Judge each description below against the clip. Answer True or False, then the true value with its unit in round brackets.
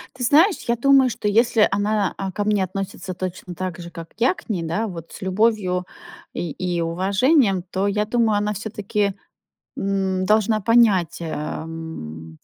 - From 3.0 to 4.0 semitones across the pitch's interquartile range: True (3.4 semitones)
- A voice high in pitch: True (195 Hz)